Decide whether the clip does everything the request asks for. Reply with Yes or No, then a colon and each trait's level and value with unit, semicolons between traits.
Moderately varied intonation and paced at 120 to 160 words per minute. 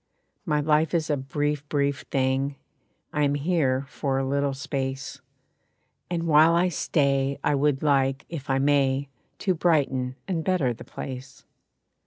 No: narrow, 2.2 semitones; average, 150 wpm